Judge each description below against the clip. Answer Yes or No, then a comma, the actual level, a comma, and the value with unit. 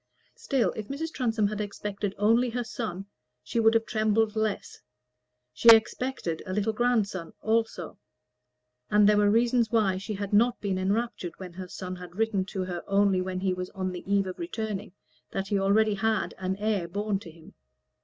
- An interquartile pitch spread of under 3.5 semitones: Yes, average, 2.9 semitones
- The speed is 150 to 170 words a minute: No, average, 185 wpm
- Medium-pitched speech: No, high, 205 Hz